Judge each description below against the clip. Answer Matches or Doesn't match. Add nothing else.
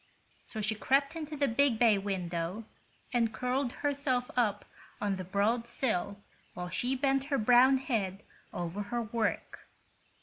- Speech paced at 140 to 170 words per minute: Matches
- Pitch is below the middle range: Doesn't match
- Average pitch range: Matches